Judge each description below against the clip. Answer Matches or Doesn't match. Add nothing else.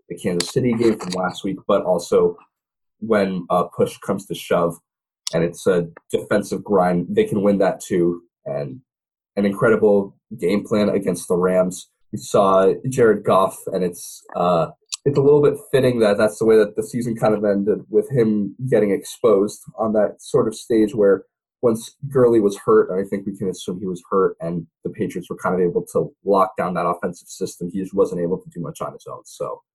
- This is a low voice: Matches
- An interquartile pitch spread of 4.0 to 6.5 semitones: Matches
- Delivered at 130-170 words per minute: Doesn't match